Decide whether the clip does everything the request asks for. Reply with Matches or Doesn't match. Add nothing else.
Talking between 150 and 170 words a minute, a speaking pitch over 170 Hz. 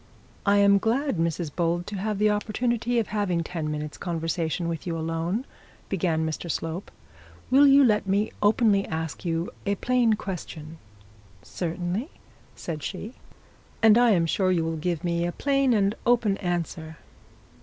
Matches